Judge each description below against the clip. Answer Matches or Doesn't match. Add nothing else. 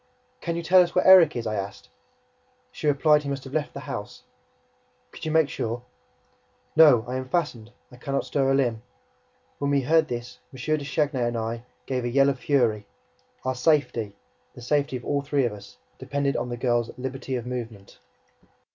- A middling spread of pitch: Matches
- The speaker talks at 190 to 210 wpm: Matches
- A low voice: Matches